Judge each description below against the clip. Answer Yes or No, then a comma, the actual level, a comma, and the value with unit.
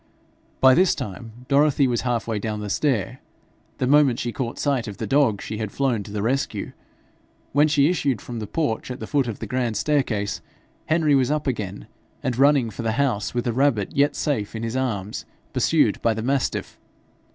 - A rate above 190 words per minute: Yes, average, 200 wpm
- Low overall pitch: Yes, low, 125 Hz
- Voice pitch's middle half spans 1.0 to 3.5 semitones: No, average, 4.2 semitones